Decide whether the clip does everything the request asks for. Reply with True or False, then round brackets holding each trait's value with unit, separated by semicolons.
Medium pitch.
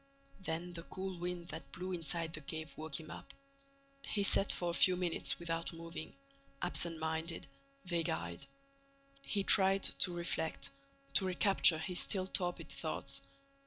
True (170 Hz)